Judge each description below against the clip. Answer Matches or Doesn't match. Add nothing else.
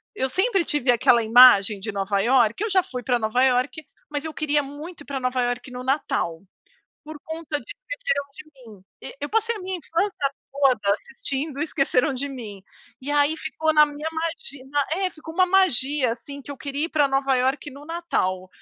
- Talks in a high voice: Matches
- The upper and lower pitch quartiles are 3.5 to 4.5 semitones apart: Matches